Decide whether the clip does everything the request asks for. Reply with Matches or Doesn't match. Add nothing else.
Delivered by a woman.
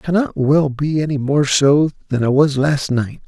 Doesn't match